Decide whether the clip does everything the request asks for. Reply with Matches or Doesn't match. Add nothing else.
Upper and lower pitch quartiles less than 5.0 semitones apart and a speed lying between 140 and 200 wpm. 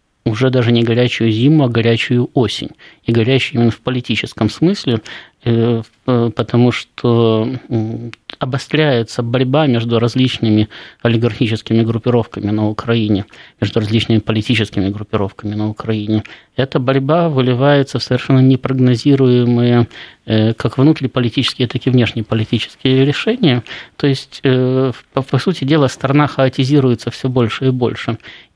Doesn't match